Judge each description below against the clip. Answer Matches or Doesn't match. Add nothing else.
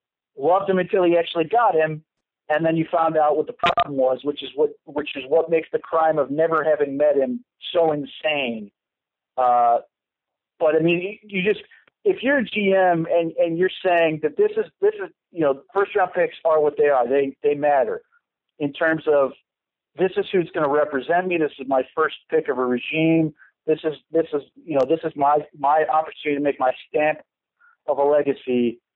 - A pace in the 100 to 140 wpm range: Doesn't match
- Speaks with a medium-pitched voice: Matches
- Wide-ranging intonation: Doesn't match